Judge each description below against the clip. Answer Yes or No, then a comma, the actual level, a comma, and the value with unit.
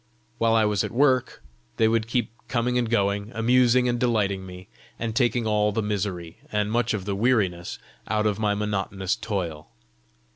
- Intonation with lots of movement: No, average, 2.9 semitones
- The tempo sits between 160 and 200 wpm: Yes, average, 175 wpm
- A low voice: Yes, low, 105 Hz